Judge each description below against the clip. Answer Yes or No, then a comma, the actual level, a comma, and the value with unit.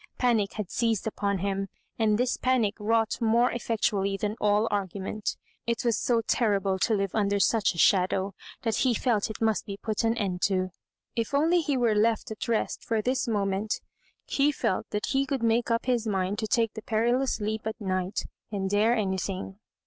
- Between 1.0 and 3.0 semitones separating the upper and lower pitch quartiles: Yes, average, 2.7 semitones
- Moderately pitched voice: No, high, 215 Hz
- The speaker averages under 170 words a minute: No, average, 190 wpm